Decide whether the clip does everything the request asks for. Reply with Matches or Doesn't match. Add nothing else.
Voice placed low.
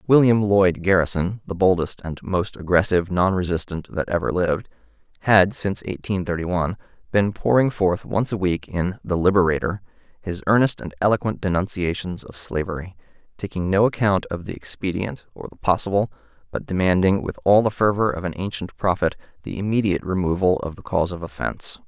Matches